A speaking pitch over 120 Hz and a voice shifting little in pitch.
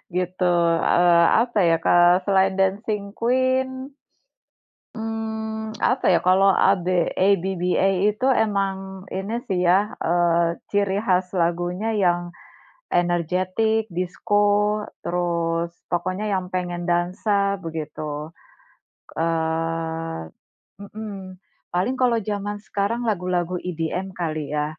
No: medium, 185 Hz; average, 3.1 semitones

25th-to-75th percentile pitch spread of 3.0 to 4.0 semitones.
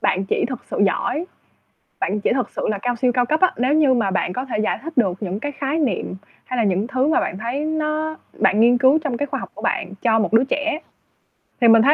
No: average, 4.7 semitones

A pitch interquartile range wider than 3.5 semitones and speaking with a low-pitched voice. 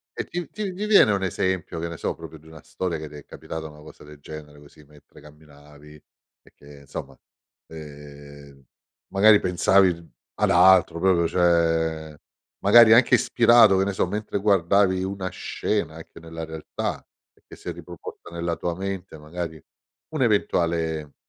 Yes: average, 4.2 semitones; very low, 85 Hz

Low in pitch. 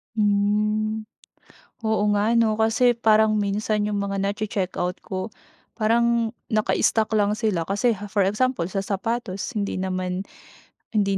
No: high, 210 Hz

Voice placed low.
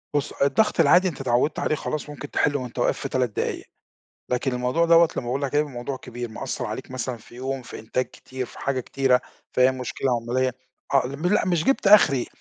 Yes: low, 130 Hz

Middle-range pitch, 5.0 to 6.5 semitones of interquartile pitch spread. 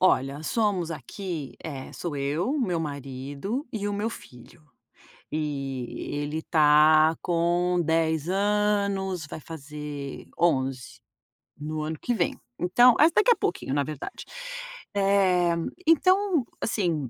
Yes: medium, 165 Hz; average, 5.3 semitones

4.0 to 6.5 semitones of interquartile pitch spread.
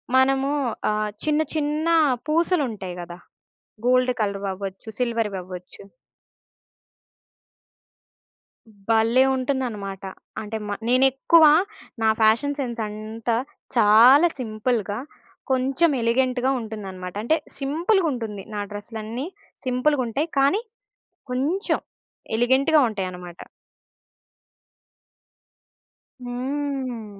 Yes: average, 4.3 semitones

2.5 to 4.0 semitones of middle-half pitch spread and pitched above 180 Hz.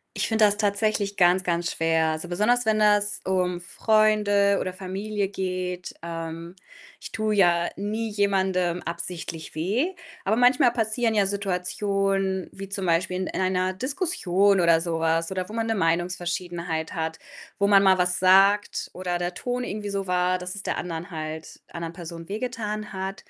Yes: average, 2.9 semitones; high, 190 Hz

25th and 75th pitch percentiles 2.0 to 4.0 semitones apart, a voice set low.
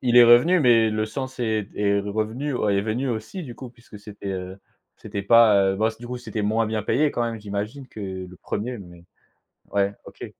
Yes: average, 3.1 semitones; low, 110 Hz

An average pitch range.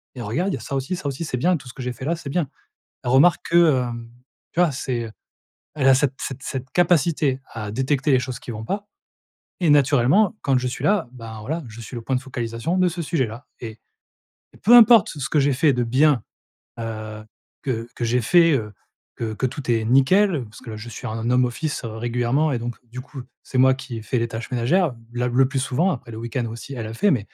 Yes: average, 4.1 semitones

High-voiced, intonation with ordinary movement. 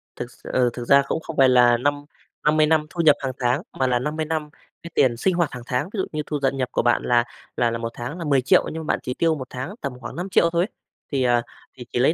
No: low, 135 Hz; average, 4.2 semitones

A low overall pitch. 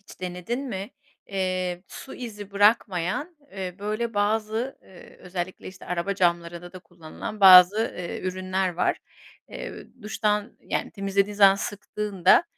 No: high, 195 Hz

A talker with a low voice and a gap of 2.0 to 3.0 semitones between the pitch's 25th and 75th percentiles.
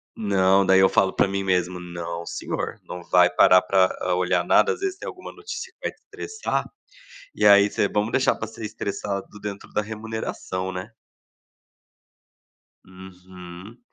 Yes: very low, 95 Hz; narrow, 2.4 semitones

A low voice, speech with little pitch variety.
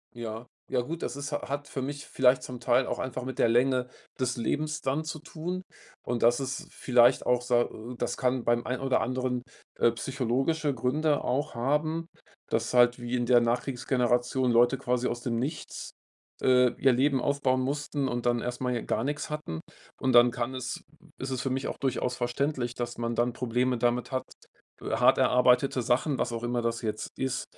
Yes: low, 125 Hz; narrow, 2.0 semitones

